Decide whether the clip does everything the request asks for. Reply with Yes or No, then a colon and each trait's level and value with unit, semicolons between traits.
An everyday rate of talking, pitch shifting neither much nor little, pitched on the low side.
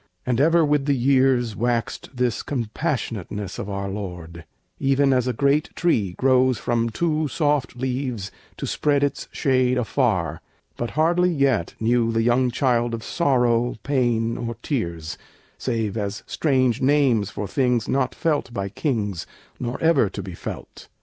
Yes: average, 150 wpm; average, 3.9 semitones; low, 125 Hz